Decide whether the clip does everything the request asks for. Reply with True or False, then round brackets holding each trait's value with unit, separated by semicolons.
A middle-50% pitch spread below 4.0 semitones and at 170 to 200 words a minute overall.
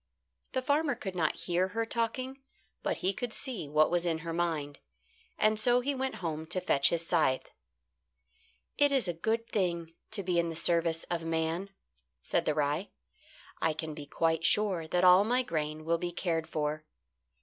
False (5.0 semitones; 180 wpm)